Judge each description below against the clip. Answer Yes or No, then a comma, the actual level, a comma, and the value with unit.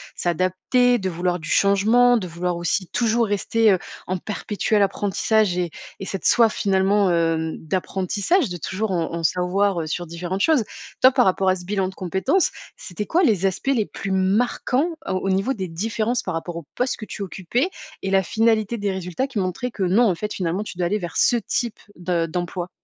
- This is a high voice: Yes, high, 195 Hz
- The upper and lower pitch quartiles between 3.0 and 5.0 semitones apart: Yes, average, 3.6 semitones